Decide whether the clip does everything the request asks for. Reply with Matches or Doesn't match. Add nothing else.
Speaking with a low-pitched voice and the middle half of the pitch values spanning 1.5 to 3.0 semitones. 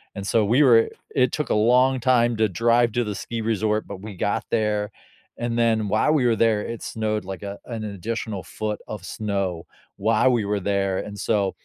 Matches